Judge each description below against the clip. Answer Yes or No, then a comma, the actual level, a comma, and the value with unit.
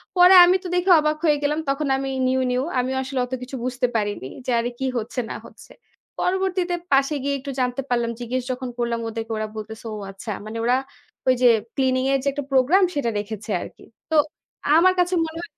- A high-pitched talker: Yes, very high, 260 Hz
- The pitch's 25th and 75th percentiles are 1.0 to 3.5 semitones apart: No, average, 4.2 semitones